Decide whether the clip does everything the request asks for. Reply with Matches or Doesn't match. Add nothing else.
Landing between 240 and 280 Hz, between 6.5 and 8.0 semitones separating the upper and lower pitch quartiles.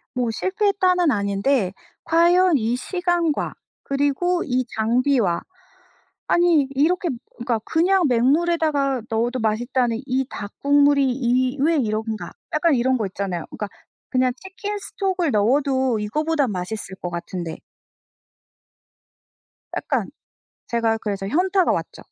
Matches